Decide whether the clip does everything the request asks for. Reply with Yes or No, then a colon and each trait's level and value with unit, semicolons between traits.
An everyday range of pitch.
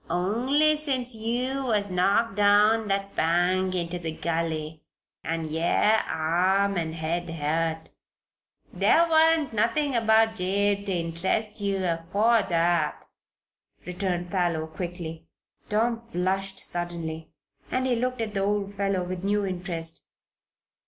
Yes: average, 4.6 semitones